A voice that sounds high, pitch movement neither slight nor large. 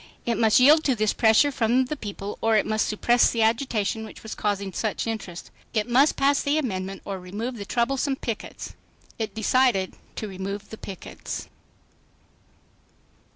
Yes: high, 220 Hz; average, 3.7 semitones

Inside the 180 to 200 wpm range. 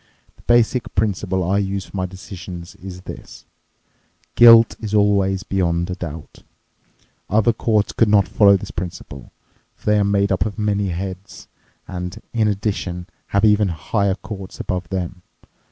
No: average, 155 wpm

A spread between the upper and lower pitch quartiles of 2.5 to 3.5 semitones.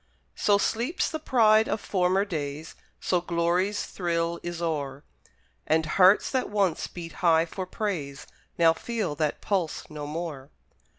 No: average, 4.0 semitones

